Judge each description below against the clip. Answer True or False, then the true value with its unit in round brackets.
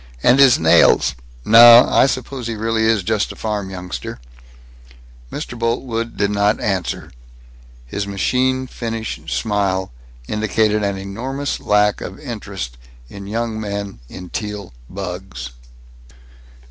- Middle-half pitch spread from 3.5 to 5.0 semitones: False (2.9 semitones)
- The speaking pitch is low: True (105 Hz)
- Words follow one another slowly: True (120 wpm)